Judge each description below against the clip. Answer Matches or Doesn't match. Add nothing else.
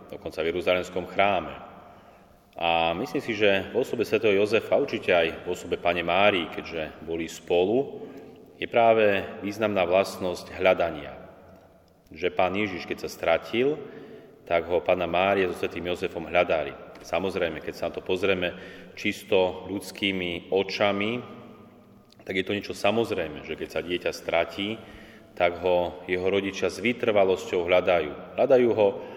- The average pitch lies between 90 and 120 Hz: Matches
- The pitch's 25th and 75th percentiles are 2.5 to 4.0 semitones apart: Doesn't match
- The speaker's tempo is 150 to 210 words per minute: Doesn't match